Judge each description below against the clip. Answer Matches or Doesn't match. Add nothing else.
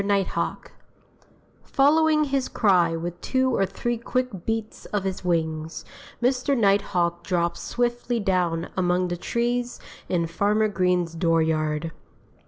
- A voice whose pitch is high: Matches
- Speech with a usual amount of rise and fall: Doesn't match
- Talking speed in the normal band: Doesn't match